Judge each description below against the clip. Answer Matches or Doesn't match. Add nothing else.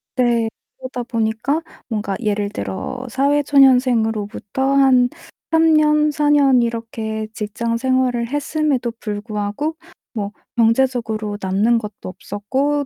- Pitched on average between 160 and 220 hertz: Doesn't match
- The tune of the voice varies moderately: Matches